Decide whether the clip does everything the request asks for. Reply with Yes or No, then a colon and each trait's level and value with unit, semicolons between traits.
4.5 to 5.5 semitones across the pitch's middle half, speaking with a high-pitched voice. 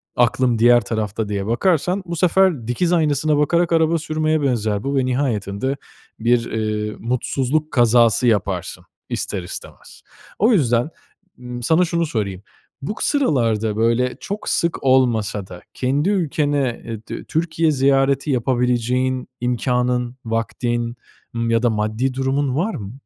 No: average, 4.8 semitones; low, 125 Hz